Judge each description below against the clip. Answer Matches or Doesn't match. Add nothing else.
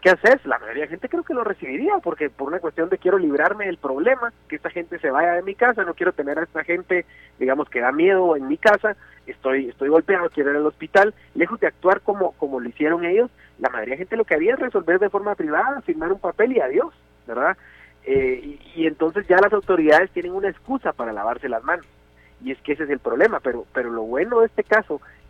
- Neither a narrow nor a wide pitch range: Doesn't match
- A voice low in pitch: Doesn't match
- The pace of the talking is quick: Matches